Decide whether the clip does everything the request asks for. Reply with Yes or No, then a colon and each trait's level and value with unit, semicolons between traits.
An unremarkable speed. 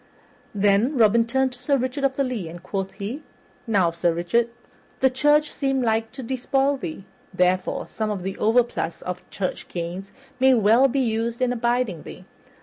Yes: average, 175 wpm